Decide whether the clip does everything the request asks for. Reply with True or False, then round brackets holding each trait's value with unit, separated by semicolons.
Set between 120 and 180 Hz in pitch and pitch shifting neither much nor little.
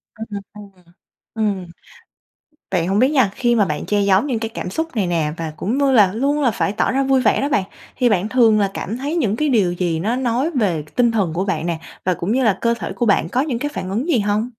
False (220 Hz; 5.0 semitones)